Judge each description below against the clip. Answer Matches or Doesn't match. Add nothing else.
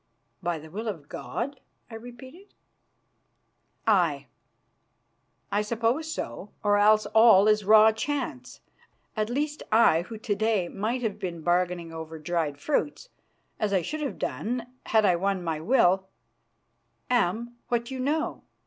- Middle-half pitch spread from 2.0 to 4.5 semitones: Doesn't match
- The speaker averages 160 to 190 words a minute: Doesn't match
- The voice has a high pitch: Matches